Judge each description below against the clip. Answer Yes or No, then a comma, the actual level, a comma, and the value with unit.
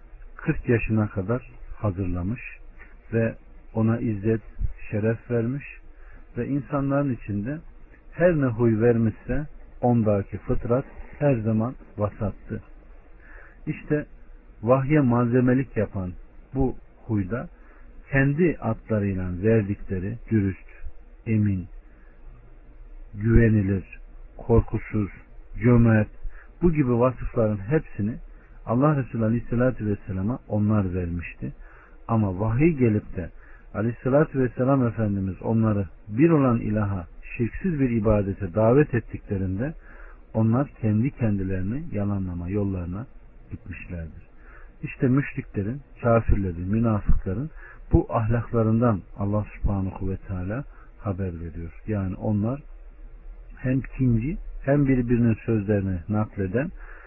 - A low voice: Yes, low, 110 Hz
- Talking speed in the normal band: No, slow, 90 wpm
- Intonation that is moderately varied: Yes, average, 4.0 semitones